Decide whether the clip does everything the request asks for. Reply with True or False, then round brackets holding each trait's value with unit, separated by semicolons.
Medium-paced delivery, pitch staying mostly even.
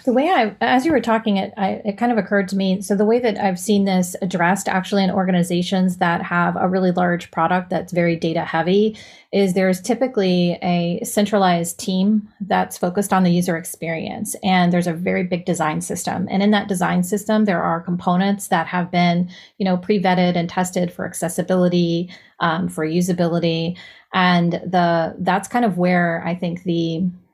True (190 wpm; 2.3 semitones)